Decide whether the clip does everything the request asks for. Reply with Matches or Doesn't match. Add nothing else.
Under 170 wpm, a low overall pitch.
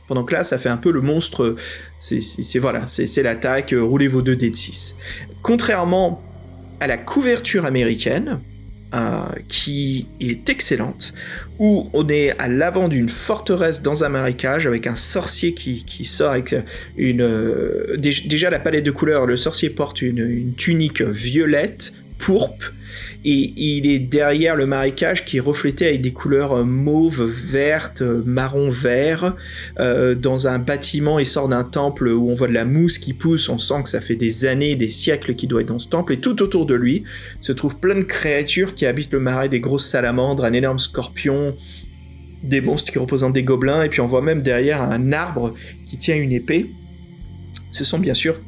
Doesn't match